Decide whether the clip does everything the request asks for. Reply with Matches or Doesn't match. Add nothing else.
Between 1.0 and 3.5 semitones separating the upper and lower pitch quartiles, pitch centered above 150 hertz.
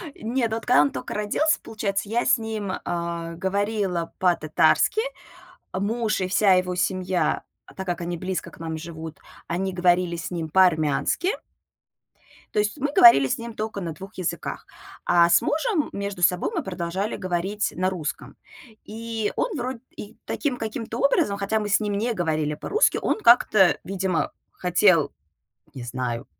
Doesn't match